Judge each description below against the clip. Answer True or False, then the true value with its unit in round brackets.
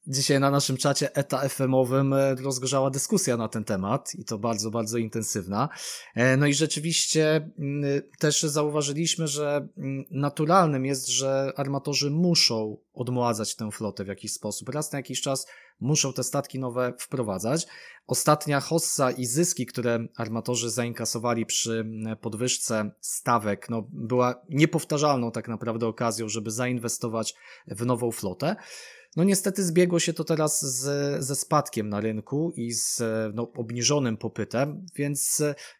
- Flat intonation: False (4.0 semitones)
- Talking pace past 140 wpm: False (135 wpm)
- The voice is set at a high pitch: False (130 Hz)